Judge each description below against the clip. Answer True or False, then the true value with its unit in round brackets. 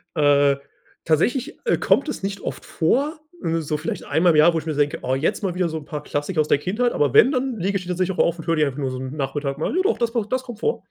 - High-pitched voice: False (165 Hz)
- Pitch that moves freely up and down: True (7.1 semitones)